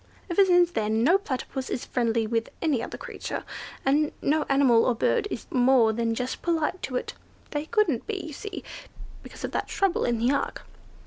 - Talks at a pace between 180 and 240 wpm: Yes, average, 190 wpm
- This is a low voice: No, very high, 270 Hz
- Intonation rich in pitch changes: Yes, wide, 6.4 semitones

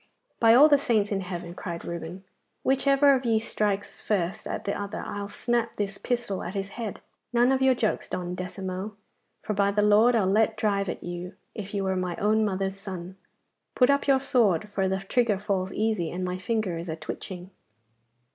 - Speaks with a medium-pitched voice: No, high, 200 Hz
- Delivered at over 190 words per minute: Yes, average, 200 wpm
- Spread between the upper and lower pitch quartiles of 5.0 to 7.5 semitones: No, average, 3.3 semitones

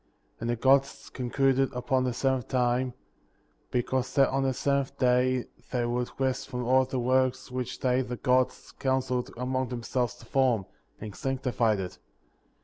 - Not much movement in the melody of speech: Yes, narrow, 1.2 semitones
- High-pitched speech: No, low, 130 Hz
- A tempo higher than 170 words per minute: No, average, 165 wpm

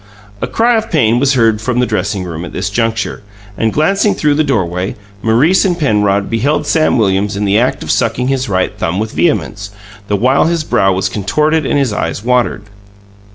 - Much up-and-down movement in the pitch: Yes, wide, 6.1 semitones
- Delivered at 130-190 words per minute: No, average, 200 wpm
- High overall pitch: No, low, 115 Hz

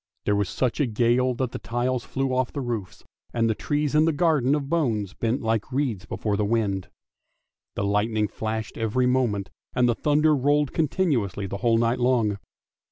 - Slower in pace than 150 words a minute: No, average, 185 wpm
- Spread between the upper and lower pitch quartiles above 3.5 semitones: Yes, average, 4.1 semitones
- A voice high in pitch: No, low, 120 Hz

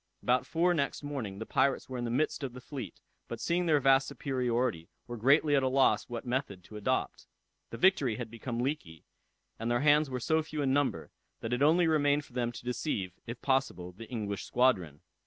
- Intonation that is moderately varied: Yes, average, 3.8 semitones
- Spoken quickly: Yes, fast, 210 wpm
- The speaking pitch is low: Yes, low, 130 Hz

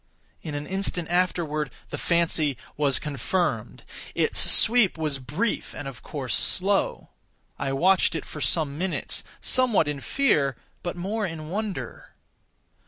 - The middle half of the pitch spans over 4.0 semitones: Yes, average, 4.7 semitones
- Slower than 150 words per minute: Yes, slow, 135 wpm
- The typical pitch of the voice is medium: Yes, medium, 160 Hz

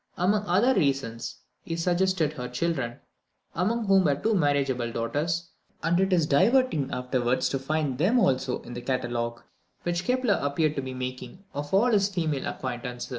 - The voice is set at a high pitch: No, medium, 150 Hz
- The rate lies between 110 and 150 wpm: No, average, 165 wpm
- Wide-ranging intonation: Yes, wide, 6.5 semitones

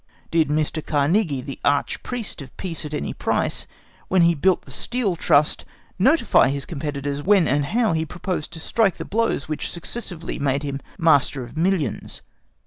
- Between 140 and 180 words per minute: Yes, average, 175 wpm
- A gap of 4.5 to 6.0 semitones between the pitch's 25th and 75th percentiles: Yes, average, 4.8 semitones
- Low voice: No, medium, 160 Hz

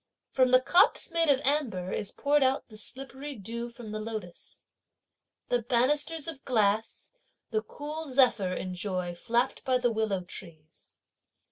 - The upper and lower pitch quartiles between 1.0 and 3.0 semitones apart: No, average, 4.8 semitones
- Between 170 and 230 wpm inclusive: No, average, 145 wpm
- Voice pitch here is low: No, high, 240 Hz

